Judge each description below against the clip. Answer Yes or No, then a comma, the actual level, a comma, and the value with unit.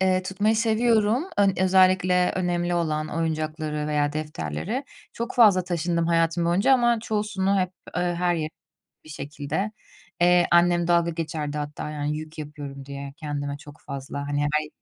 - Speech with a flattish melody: No, average, 3.8 semitones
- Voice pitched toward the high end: No, medium, 170 Hz